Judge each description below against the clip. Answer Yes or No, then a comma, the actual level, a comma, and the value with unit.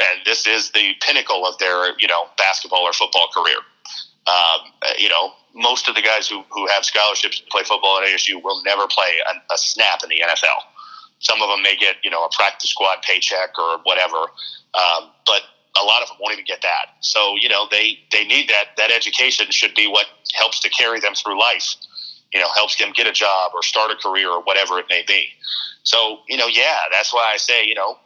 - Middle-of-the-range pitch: No, low, 105 Hz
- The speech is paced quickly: Yes, fast, 225 wpm